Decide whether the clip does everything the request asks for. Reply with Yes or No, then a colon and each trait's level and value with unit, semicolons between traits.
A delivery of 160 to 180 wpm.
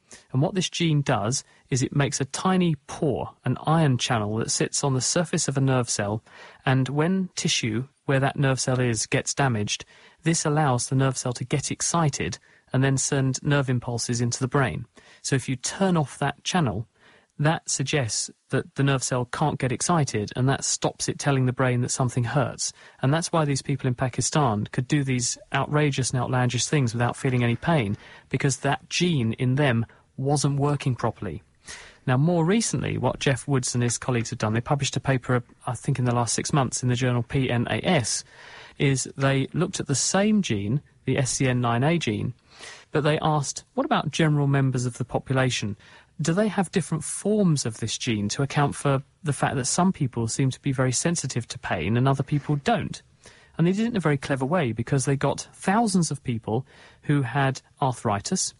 No: average, 195 wpm